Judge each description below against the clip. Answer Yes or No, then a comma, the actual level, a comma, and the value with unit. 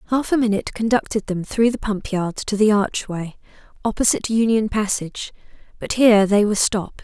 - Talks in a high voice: Yes, high, 210 Hz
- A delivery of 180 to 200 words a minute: No, average, 170 wpm